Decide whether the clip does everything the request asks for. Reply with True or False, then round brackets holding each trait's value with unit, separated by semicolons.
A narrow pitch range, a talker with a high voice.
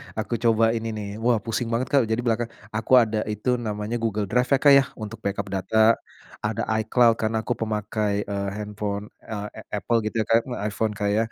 False (1.7 semitones; 110 Hz)